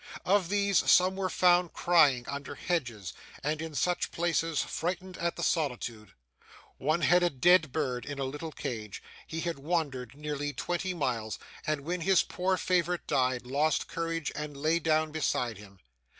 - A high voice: No, medium, 155 Hz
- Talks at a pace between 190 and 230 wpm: No, average, 165 wpm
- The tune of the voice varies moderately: Yes, average, 4.4 semitones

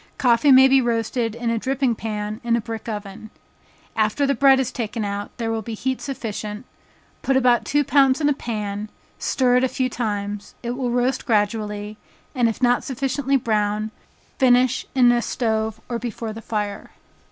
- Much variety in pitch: No, average, 3.2 semitones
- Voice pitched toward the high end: Yes, high, 235 Hz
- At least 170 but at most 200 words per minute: Yes, average, 180 wpm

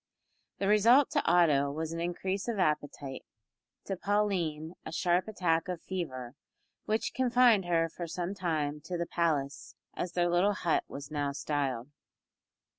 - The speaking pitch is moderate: Yes, medium, 170 Hz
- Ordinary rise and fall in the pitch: Yes, average, 4.2 semitones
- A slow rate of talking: No, average, 150 wpm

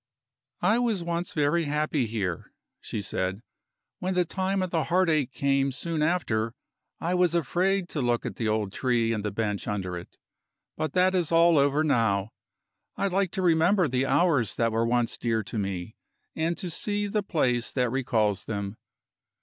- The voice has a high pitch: No, medium, 140 Hz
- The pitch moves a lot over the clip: Yes, wide, 7.5 semitones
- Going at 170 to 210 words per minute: Yes, average, 175 wpm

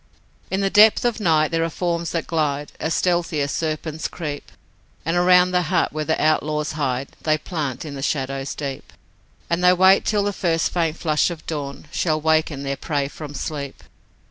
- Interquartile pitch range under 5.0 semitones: Yes, average, 2.9 semitones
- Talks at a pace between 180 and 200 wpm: Yes, average, 190 wpm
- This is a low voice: No, medium, 155 Hz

